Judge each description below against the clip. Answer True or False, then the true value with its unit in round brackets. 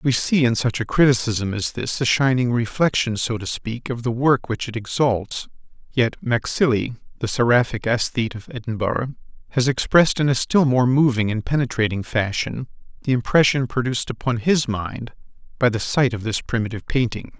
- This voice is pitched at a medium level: False (120 Hz)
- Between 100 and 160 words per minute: False (170 wpm)